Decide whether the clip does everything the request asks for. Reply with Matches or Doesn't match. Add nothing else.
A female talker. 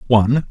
Doesn't match